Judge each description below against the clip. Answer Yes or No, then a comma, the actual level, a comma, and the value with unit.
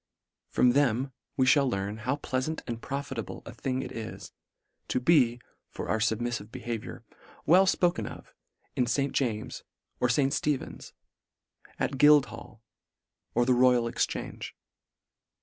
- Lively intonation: No, average, 3.0 semitones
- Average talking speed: No, slow, 130 wpm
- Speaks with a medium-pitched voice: No, low, 125 Hz